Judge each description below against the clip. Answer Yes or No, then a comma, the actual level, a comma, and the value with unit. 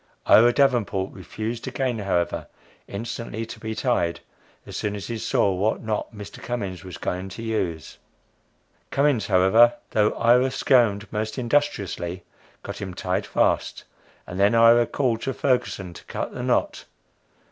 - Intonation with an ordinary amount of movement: Yes, average, 3.8 semitones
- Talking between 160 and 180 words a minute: No, average, 145 wpm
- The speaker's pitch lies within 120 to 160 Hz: No, low, 110 Hz